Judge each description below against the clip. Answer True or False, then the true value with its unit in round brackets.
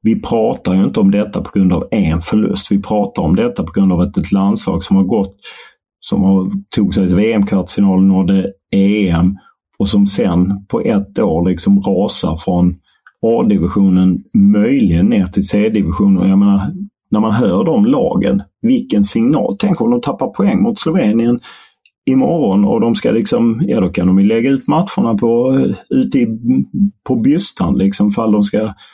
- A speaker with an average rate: True (175 wpm)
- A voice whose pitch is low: True (105 Hz)